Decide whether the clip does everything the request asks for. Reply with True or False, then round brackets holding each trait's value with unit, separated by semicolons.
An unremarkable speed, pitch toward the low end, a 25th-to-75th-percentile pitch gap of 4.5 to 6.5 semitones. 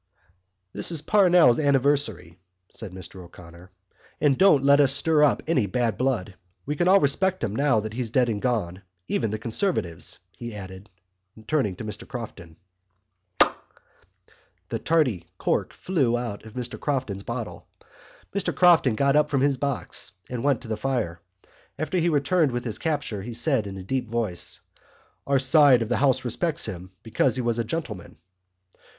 True (165 wpm; 125 Hz; 5.3 semitones)